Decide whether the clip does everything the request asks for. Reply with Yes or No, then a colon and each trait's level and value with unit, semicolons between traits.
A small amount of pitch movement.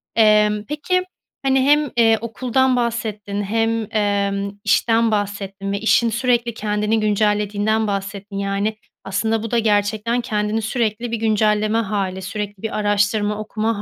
Yes: narrow, 1.8 semitones